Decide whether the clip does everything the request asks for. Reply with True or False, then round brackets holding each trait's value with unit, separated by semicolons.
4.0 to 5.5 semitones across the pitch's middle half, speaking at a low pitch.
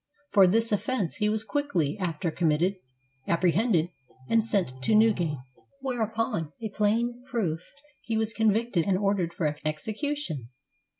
False (5.1 semitones; 205 Hz)